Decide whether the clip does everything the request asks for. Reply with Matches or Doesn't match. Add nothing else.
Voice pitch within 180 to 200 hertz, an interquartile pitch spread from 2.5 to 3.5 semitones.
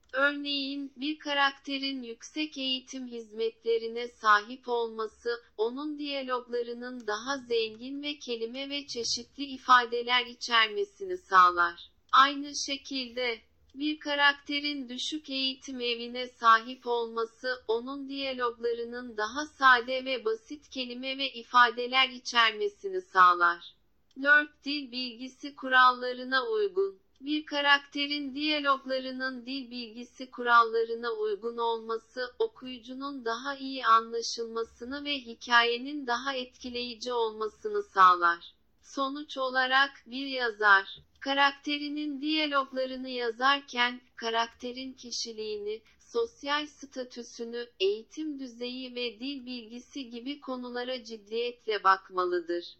Doesn't match